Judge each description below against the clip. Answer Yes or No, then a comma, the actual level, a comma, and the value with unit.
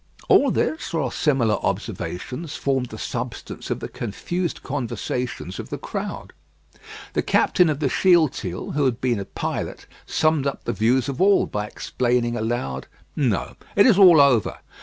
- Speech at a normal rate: Yes, average, 160 wpm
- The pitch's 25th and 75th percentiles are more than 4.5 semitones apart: Yes, average, 4.9 semitones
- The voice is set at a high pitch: No, low, 130 Hz